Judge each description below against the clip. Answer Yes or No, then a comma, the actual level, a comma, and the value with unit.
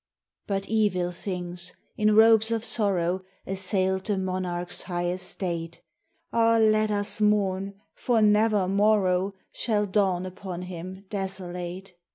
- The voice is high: Yes, high, 195 Hz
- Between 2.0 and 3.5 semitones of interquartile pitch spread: Yes, narrow, 2.6 semitones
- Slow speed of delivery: Yes, slow, 120 wpm